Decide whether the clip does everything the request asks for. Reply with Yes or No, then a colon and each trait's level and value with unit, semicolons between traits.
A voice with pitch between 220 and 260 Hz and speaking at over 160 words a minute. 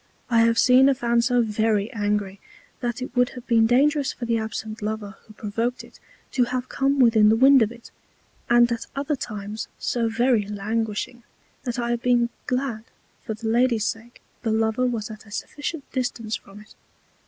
Yes: high, 235 Hz; average, 190 wpm